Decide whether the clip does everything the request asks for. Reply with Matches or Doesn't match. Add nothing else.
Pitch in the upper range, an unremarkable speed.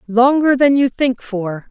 Matches